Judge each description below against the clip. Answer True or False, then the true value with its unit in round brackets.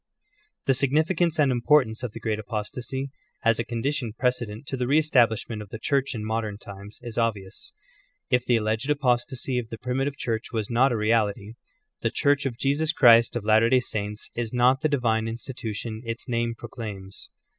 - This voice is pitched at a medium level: False (120 Hz)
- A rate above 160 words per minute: True (190 wpm)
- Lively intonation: False (3.1 semitones)